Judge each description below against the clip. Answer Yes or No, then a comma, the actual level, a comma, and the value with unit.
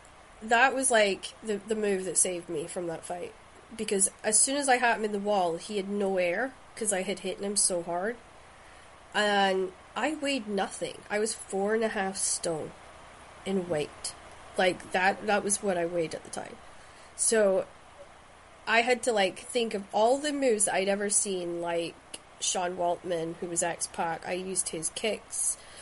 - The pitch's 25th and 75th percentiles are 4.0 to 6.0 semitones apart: No, average, 3.5 semitones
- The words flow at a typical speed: Yes, average, 185 wpm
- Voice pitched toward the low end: No, high, 200 Hz